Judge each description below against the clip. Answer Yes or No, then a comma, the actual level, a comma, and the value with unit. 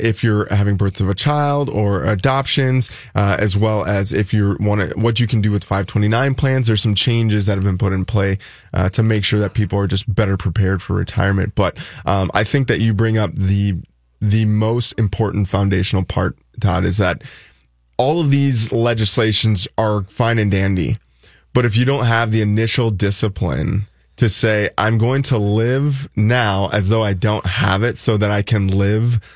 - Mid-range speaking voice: No, low, 105 Hz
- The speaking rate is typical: Yes, average, 195 wpm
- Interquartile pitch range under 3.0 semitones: Yes, narrow, 2.5 semitones